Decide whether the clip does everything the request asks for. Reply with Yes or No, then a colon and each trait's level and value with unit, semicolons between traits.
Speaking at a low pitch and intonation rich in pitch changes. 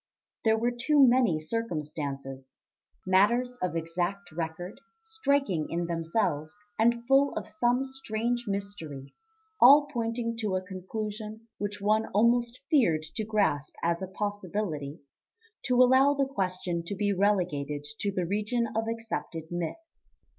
No: high, 205 Hz; wide, 5.7 semitones